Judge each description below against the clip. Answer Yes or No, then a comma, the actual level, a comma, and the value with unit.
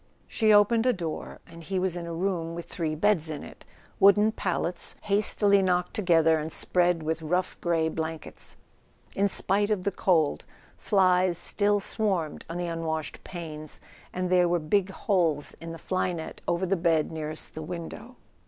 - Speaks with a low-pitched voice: No, medium, 175 Hz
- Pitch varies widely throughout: No, average, 3.2 semitones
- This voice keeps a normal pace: Yes, average, 170 wpm